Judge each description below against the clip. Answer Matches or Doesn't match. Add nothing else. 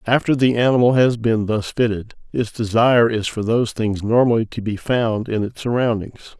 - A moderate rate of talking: Matches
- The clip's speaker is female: Doesn't match